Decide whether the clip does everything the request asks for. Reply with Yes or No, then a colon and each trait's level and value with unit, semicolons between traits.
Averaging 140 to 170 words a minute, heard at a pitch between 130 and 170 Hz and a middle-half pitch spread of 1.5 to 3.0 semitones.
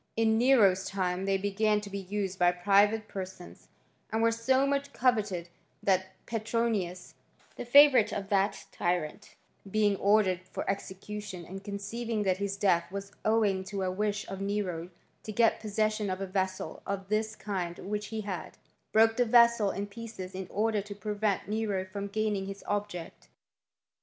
No: average, 165 wpm; high, 200 Hz; narrow, 2.4 semitones